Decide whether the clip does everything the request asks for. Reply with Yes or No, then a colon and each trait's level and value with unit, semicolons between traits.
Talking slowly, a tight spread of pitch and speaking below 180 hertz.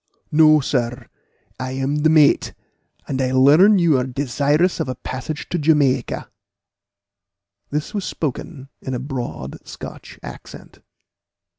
No: slow, 130 wpm; average, 3.0 semitones; medium, 140 Hz